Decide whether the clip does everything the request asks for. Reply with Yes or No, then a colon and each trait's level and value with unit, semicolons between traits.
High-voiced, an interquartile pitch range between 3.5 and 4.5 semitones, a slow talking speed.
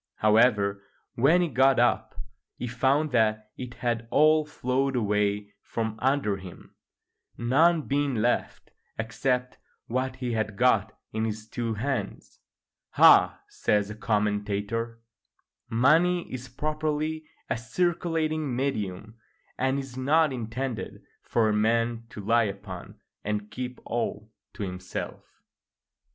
No: low, 120 Hz; average, 4.1 semitones; slow, 120 wpm